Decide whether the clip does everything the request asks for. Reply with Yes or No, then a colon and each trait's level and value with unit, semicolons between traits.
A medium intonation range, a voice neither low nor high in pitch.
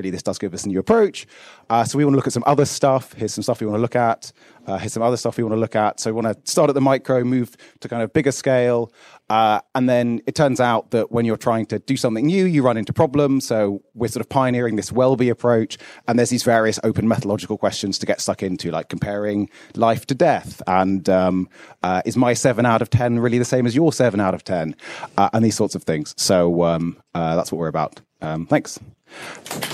No: average, 3.5 semitones; low, 115 Hz